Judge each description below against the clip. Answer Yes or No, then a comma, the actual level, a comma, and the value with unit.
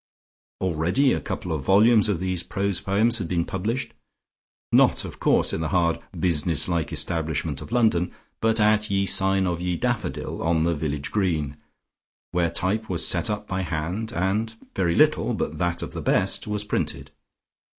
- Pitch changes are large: No, average, 4.0 semitones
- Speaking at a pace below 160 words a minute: No, average, 170 wpm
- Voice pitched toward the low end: Yes, very low, 95 Hz